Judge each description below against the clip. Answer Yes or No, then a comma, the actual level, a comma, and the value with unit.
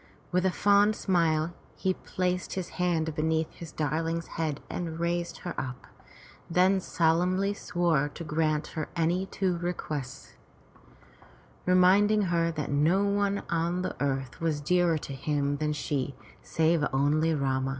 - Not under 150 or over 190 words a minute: No, average, 140 wpm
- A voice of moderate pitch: Yes, medium, 165 Hz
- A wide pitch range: No, average, 3.1 semitones